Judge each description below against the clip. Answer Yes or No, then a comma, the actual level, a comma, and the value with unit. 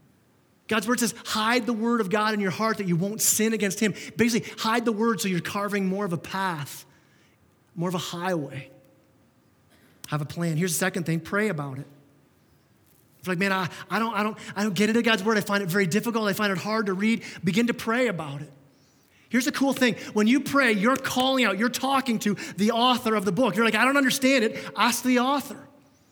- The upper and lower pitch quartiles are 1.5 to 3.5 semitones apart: No, average, 4.0 semitones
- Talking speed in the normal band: No, fast, 230 wpm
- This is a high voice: Yes, high, 215 Hz